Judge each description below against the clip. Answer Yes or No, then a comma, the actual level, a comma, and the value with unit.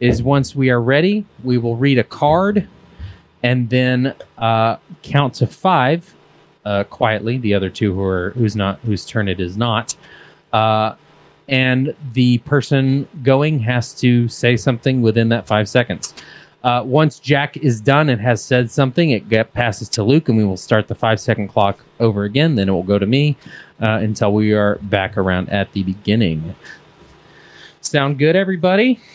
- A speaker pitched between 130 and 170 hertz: No, low, 120 Hz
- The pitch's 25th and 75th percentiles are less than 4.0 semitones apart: No, average, 4.6 semitones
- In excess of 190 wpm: No, average, 175 wpm